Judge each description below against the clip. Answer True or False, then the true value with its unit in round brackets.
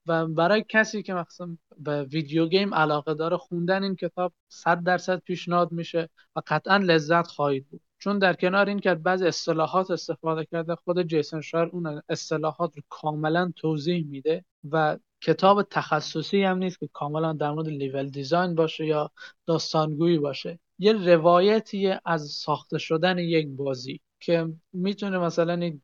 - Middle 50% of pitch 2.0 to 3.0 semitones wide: True (2.5 semitones)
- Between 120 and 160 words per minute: True (150 wpm)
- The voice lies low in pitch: False (170 Hz)